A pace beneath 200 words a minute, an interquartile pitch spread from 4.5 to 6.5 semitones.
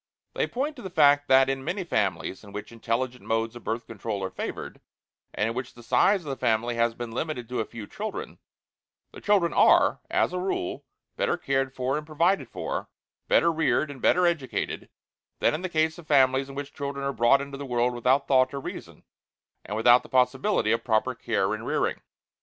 No: fast, 205 wpm; average, 4.8 semitones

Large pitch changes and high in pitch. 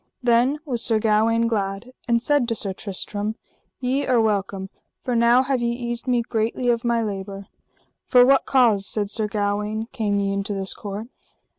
No: average, 3.0 semitones; high, 225 Hz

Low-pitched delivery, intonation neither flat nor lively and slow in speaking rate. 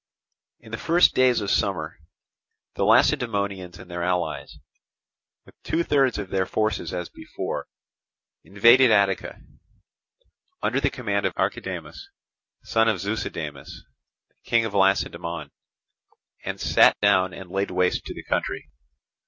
Yes: low, 100 Hz; average, 3.9 semitones; slow, 125 wpm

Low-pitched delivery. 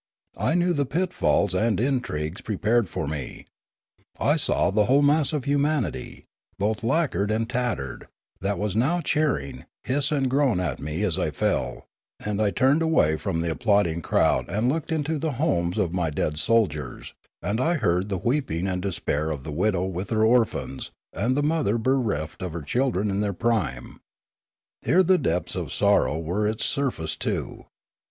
Yes: low, 105 Hz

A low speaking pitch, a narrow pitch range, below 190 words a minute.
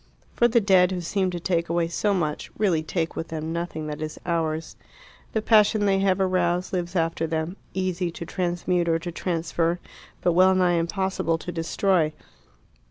No: medium, 175 Hz; narrow, 2.3 semitones; average, 175 wpm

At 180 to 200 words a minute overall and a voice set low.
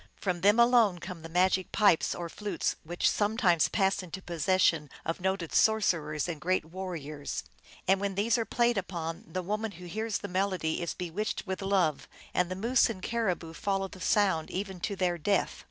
No: average, 185 wpm; medium, 185 Hz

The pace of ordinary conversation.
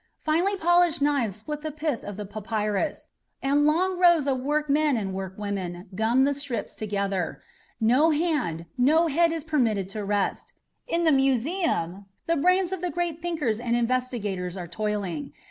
Yes: average, 160 wpm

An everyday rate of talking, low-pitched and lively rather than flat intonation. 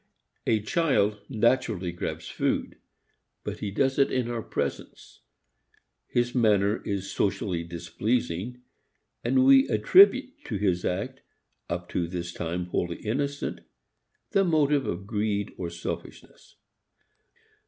No: slow, 120 wpm; low, 105 Hz; wide, 6.5 semitones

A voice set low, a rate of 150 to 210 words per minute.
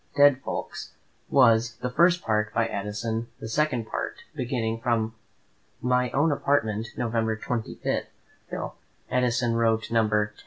No: low, 115 Hz; average, 140 wpm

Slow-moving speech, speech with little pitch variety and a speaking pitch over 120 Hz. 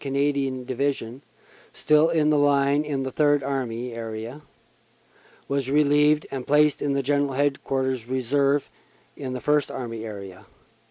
Yes: slow, 130 wpm; narrow, 2.3 semitones; medium, 140 Hz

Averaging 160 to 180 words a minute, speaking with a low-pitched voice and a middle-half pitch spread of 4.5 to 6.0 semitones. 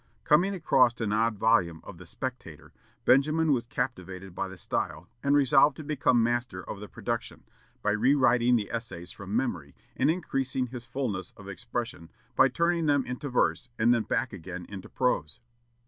Yes: average, 170 wpm; low, 120 Hz; average, 5.3 semitones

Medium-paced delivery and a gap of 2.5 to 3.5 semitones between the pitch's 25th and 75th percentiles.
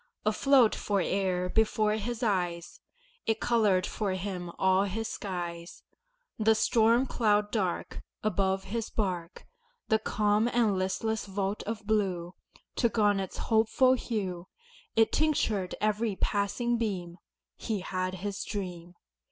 No: slow, 125 wpm; average, 3.0 semitones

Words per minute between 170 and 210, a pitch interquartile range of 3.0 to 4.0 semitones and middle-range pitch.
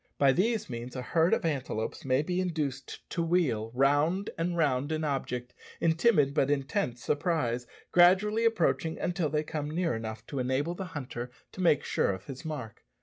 No: average, 180 wpm; average, 5.0 semitones; medium, 150 Hz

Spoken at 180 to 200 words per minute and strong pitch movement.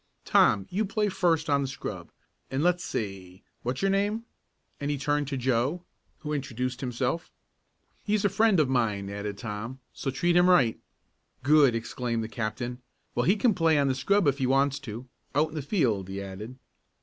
Yes: average, 185 wpm; wide, 6.1 semitones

